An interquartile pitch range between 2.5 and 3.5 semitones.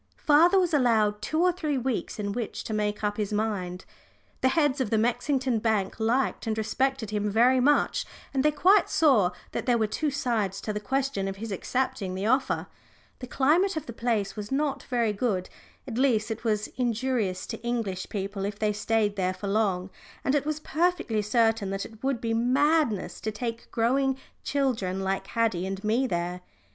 No: average, 4.4 semitones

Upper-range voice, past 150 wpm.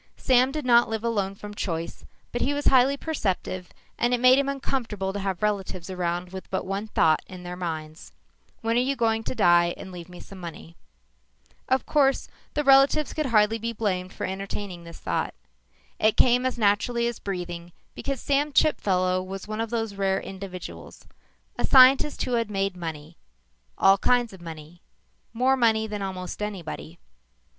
Yes: high, 205 Hz; average, 175 wpm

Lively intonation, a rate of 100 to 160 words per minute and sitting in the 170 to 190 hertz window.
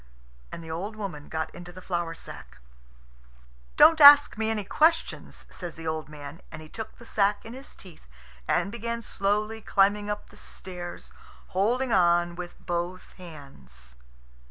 No: average, 4.7 semitones; average, 155 wpm; medium, 185 Hz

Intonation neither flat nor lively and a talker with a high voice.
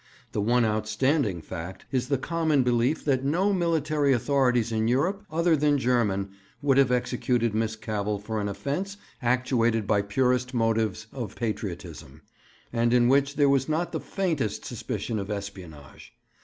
No: average, 4.7 semitones; low, 125 Hz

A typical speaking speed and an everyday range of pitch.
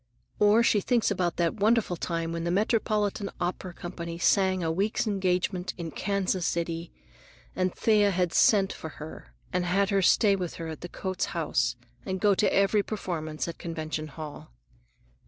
Yes: average, 165 wpm; average, 3.1 semitones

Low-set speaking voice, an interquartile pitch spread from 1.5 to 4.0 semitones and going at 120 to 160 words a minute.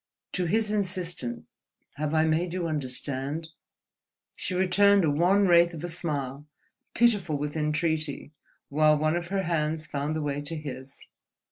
No: medium, 160 Hz; average, 3.2 semitones; average, 150 wpm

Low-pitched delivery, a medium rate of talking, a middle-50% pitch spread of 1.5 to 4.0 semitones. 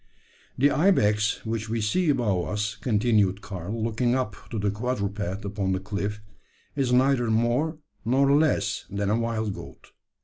Yes: low, 110 Hz; average, 150 wpm; average, 3.4 semitones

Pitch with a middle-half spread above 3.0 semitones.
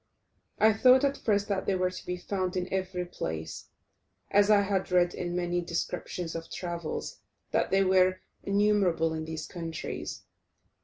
No: narrow, 2.5 semitones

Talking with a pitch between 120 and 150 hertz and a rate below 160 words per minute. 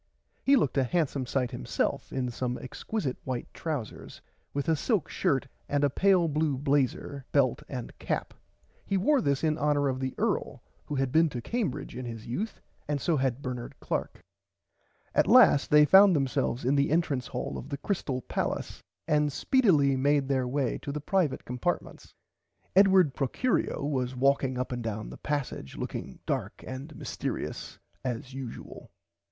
No: medium, 140 Hz; average, 165 wpm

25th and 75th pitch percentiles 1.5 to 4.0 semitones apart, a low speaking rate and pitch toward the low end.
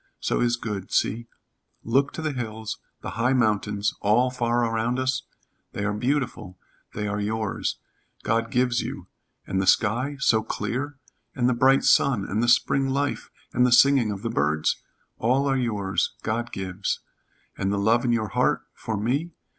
No: average, 3.5 semitones; average, 170 wpm; low, 115 Hz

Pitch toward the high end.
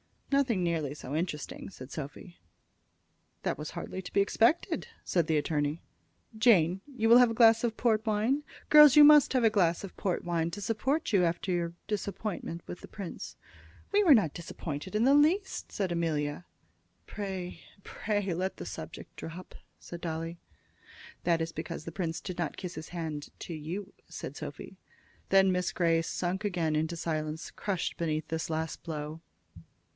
No: medium, 175 Hz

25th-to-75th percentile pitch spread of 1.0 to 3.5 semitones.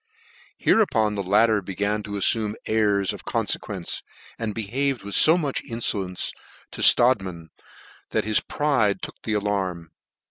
Yes: narrow, 2.5 semitones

